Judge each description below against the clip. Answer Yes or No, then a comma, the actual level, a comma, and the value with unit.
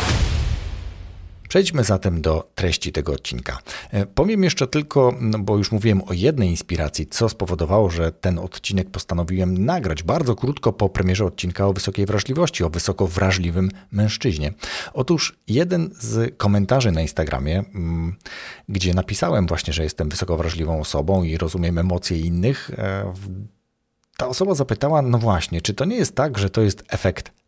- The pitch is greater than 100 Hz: No, very low, 95 Hz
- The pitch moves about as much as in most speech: Yes, average, 4.5 semitones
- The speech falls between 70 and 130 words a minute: No, average, 145 wpm